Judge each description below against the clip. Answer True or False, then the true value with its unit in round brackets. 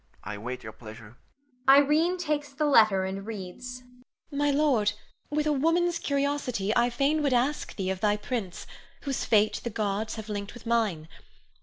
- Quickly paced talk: False (165 wpm)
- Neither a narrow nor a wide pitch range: False (6.4 semitones)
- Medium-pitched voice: False (235 Hz)